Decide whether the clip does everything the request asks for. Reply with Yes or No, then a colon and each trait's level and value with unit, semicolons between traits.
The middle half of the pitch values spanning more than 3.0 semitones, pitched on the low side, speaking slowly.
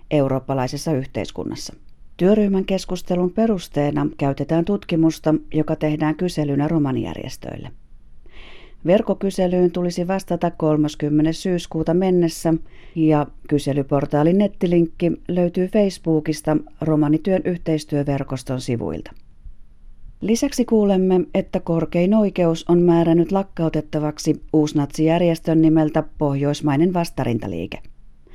No: average, 3.4 semitones; medium, 160 Hz; slow, 80 wpm